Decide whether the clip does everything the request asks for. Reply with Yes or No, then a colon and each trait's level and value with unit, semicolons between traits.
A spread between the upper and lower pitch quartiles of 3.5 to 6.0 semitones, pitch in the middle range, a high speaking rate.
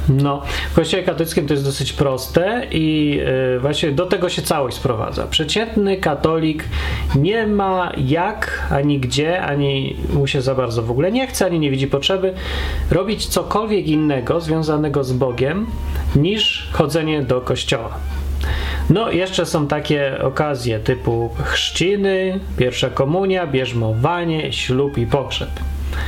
No: wide, 5.4 semitones; medium, 145 Hz; average, 135 wpm